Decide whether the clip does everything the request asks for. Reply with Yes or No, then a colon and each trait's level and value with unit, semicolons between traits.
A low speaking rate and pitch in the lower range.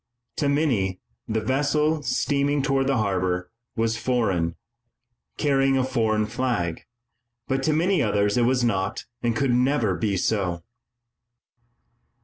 Yes: slow, 125 wpm; low, 120 Hz